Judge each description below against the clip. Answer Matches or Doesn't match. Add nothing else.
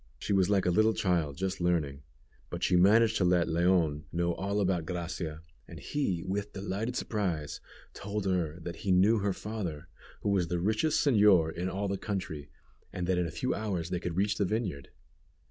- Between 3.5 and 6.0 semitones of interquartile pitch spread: Doesn't match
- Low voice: Matches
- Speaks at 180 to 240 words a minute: Matches